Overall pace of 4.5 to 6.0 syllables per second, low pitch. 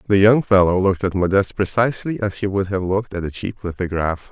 No: 6.4 syllables/s; low, 100 Hz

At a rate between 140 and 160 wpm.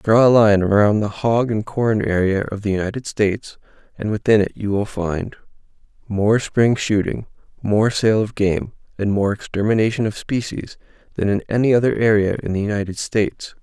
No: average, 175 wpm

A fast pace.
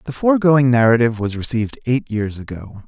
No: average, 165 wpm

